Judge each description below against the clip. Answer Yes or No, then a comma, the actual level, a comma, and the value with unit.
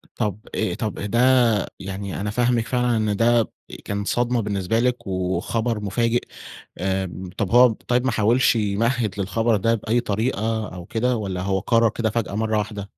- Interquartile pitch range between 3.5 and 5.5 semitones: No, average, 2.9 semitones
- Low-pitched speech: Yes, low, 110 Hz